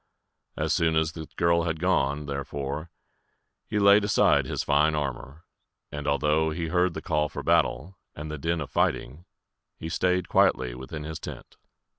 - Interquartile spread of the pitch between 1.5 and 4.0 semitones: Yes, average, 2.7 semitones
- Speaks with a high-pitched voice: No, very low, 80 Hz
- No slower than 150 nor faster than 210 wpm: Yes, average, 165 wpm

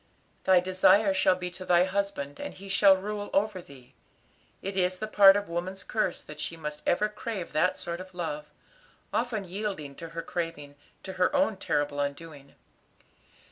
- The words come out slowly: No, average, 170 wpm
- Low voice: No, medium, 185 Hz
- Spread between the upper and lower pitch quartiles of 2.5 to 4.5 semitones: Yes, average, 3.2 semitones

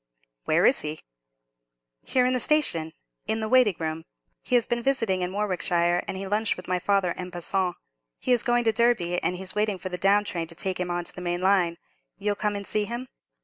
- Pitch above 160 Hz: Yes, high, 190 Hz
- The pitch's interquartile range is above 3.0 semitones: Yes, average, 3.9 semitones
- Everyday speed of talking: No, fast, 220 wpm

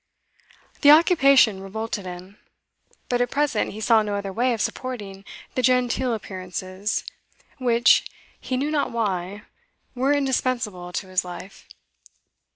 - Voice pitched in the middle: No, high, 225 Hz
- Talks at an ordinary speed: No, slow, 130 wpm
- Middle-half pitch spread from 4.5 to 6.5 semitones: Yes, average, 4.8 semitones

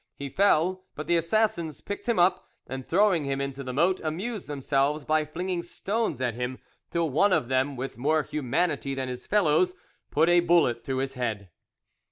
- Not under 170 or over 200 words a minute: Yes, average, 185 wpm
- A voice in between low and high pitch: Yes, medium, 155 Hz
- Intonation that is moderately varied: Yes, average, 5.0 semitones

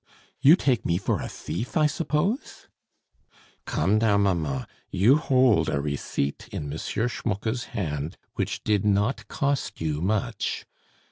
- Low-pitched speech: Yes, low, 105 Hz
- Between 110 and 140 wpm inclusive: Yes, slow, 135 wpm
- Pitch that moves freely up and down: Yes, wide, 7.3 semitones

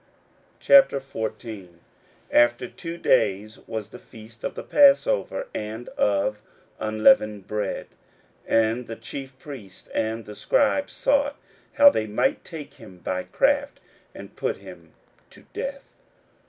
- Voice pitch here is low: Yes, low, 115 Hz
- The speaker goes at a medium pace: No, slow, 125 wpm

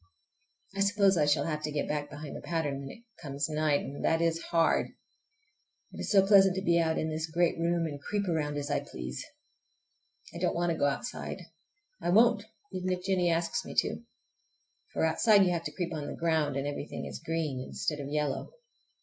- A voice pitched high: No, medium, 165 Hz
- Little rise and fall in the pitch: No, average, 3.3 semitones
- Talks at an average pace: No, fast, 210 wpm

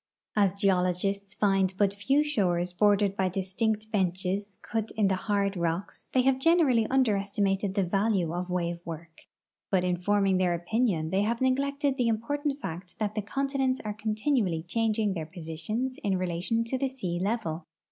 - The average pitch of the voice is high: Yes, high, 200 Hz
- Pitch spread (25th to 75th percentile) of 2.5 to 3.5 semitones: No, average, 3.9 semitones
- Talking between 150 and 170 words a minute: Yes, average, 165 wpm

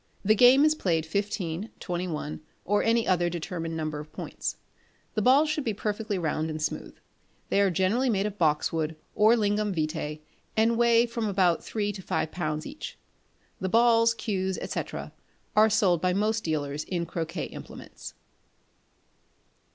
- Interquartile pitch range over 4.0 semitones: Yes, average, 5.2 semitones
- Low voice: No, high, 195 Hz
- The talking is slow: No, average, 155 wpm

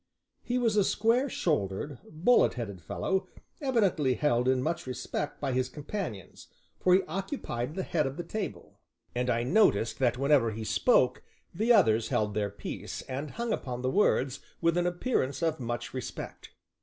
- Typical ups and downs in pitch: No, wide, 7.5 semitones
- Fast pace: No, average, 170 wpm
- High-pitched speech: No, medium, 145 Hz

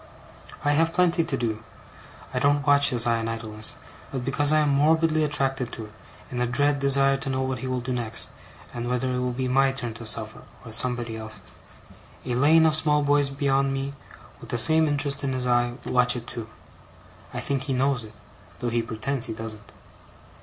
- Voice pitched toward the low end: Yes, low, 130 Hz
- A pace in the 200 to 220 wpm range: Yes, fast, 205 wpm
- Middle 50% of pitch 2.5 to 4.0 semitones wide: Yes, average, 3.1 semitones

